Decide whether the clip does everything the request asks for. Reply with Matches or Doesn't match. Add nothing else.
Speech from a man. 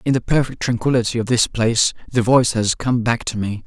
Matches